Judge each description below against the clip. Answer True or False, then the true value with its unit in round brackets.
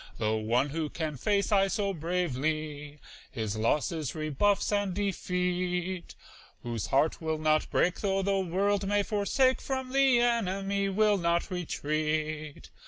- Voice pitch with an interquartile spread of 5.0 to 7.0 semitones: False (4.5 semitones)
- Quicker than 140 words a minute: False (135 wpm)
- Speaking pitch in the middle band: True (180 Hz)